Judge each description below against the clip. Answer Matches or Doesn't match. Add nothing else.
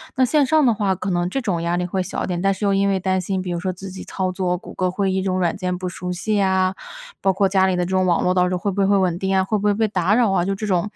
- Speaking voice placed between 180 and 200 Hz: Matches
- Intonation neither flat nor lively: Doesn't match